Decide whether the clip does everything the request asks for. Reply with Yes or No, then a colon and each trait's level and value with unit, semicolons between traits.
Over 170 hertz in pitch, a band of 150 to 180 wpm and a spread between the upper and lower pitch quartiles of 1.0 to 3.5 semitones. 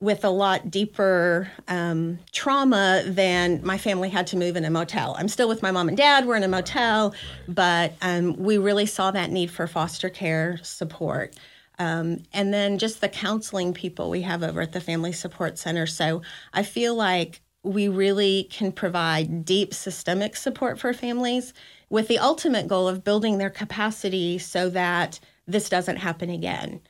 Yes: high, 190 Hz; average, 175 wpm; average, 2.9 semitones